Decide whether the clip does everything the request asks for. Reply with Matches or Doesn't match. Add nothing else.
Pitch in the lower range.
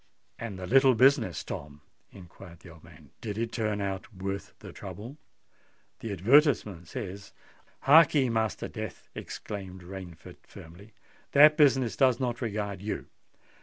Matches